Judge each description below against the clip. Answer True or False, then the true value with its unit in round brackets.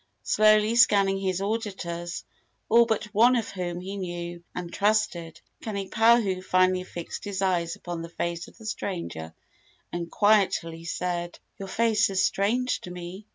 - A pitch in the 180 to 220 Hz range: True (190 Hz)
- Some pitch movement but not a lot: True (3.6 semitones)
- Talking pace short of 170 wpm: True (150 wpm)